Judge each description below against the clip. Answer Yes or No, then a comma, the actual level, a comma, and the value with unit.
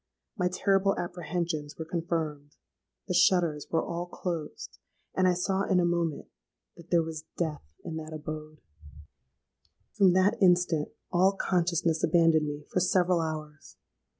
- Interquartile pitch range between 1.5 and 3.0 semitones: Yes, narrow, 2.5 semitones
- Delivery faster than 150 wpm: No, average, 140 wpm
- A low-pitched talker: No, medium, 170 Hz